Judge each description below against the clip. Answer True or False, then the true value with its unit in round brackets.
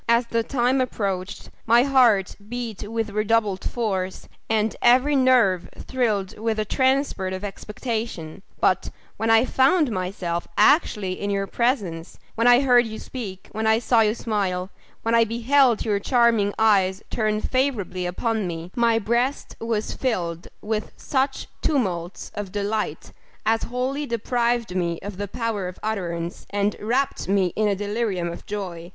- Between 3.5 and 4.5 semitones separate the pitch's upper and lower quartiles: True (3.8 semitones)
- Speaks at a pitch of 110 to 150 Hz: False (220 Hz)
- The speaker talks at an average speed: True (155 wpm)